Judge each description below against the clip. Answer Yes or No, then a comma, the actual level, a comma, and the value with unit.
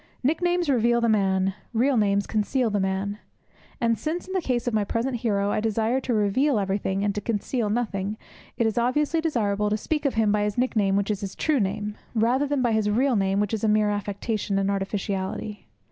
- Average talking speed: No, fast, 210 wpm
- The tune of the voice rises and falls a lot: No, average, 3.4 semitones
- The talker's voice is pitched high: Yes, high, 215 Hz